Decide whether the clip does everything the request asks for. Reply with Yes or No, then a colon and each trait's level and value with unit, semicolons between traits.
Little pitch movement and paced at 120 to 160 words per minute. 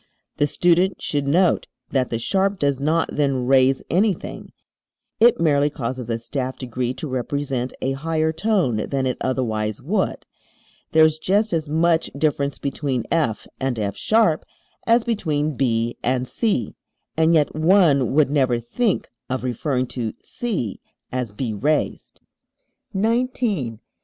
No: average, 4.7 semitones; average, 140 wpm